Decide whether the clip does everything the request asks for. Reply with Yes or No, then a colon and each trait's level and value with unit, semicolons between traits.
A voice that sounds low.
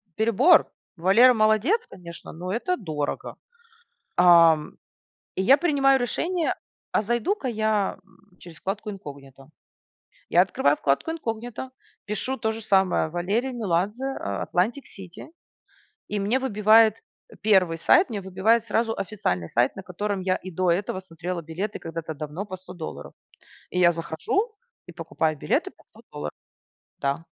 No: high, 195 Hz